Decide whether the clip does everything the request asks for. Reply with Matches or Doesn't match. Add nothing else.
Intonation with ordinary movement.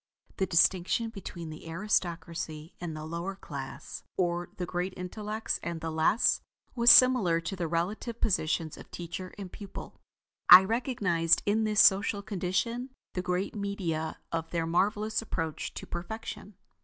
Matches